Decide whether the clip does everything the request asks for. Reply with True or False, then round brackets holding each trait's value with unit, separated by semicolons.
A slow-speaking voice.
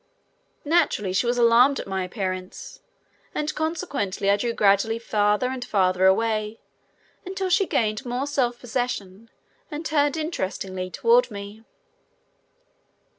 True (125 wpm)